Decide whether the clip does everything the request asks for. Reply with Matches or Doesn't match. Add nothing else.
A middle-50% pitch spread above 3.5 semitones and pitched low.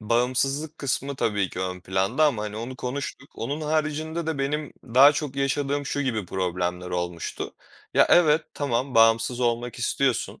Matches